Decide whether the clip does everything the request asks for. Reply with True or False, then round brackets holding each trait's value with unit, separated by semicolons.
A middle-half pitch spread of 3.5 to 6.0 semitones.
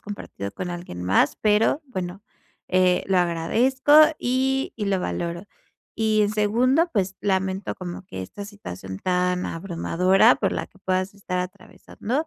False (3.1 semitones)